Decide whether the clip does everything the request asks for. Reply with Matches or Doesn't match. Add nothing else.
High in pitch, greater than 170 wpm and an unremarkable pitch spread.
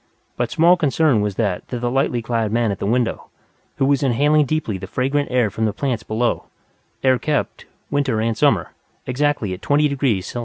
Doesn't match